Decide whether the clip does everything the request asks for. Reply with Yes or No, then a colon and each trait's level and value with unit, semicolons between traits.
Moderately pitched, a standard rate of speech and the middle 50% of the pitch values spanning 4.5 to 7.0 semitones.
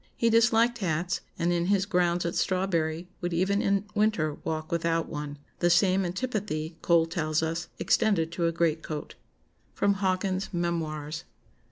No: medium, 175 Hz; average, 150 wpm; average, 3.2 semitones